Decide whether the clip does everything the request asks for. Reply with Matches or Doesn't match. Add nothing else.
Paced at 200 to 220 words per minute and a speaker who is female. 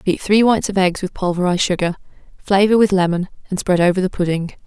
Matches